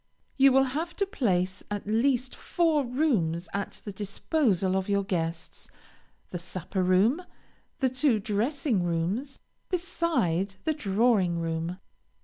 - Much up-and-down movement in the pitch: Yes, wide, 7.0 semitones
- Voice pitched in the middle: No, high, 205 Hz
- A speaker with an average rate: No, slow, 130 wpm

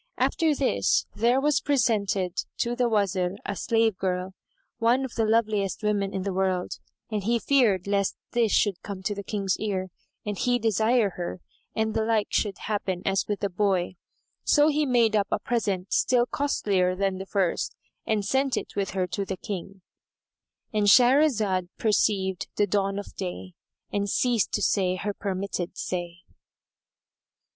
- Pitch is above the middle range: Yes, high, 205 Hz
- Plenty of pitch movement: No, average, 3.2 semitones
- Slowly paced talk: No, average, 165 wpm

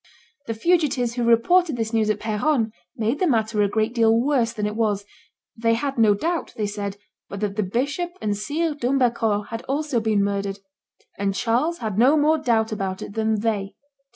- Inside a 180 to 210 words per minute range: Yes, average, 190 wpm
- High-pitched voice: Yes, high, 225 Hz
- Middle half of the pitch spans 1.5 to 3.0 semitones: No, average, 4.2 semitones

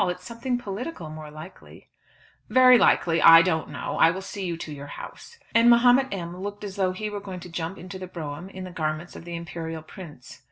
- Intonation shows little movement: No, average, 3.9 semitones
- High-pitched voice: No, medium, 180 Hz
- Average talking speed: No, fast, 215 wpm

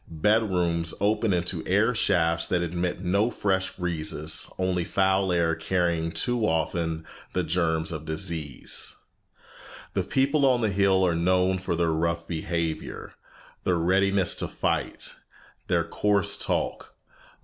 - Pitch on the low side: Yes, very low, 90 Hz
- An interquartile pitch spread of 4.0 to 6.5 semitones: No, average, 2.7 semitones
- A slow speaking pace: Yes, slow, 130 wpm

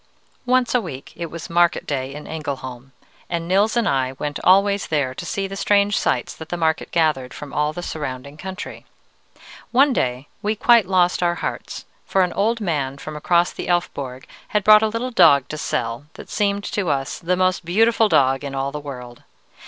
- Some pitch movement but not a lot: No, wide, 6.2 semitones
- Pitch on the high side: No, medium, 170 Hz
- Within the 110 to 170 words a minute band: No, average, 195 wpm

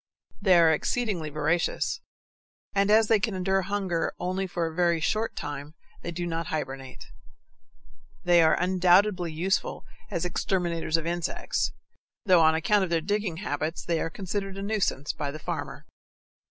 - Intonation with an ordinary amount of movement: Yes, average, 3.1 semitones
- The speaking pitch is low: No, medium, 175 Hz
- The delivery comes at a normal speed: Yes, average, 155 wpm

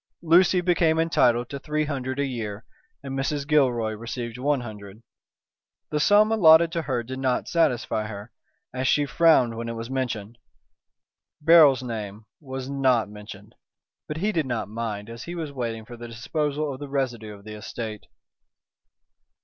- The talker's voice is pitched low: Yes, low, 130 Hz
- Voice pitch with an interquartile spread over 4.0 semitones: Yes, average, 4.8 semitones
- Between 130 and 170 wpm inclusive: Yes, average, 165 wpm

